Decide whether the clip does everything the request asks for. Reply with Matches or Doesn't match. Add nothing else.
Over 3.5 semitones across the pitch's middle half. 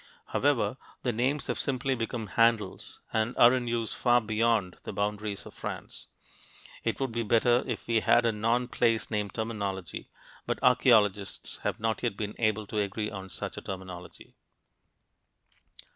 Doesn't match